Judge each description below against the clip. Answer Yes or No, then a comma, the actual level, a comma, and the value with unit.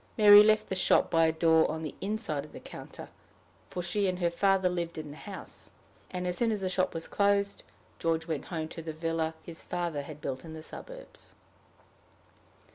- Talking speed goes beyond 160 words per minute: Yes, average, 200 wpm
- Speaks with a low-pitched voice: No, medium, 170 Hz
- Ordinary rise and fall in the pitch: Yes, average, 3.4 semitones